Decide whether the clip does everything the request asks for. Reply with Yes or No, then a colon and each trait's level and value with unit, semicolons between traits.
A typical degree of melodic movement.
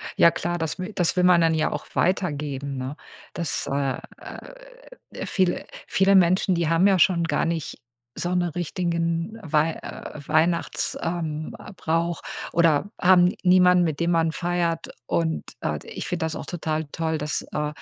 No: narrow, 2.3 semitones